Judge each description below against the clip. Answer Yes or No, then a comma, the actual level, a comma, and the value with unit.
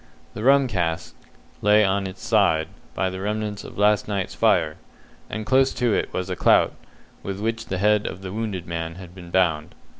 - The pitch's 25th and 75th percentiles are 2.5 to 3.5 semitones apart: Yes, average, 2.9 semitones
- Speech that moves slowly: No, average, 190 wpm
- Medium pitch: No, very low, 95 Hz